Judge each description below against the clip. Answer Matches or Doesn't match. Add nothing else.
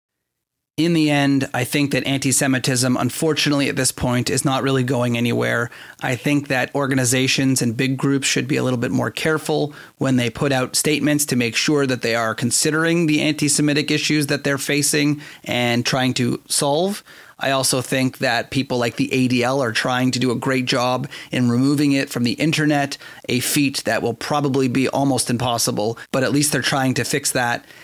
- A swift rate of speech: Doesn't match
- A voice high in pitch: Doesn't match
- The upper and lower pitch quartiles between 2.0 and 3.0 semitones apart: Matches